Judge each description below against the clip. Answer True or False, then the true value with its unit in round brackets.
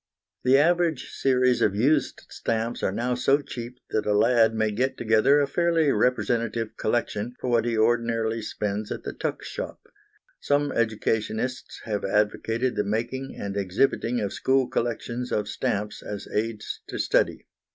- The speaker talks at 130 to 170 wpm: True (155 wpm)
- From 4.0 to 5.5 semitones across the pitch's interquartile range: False (2.9 semitones)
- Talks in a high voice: False (115 Hz)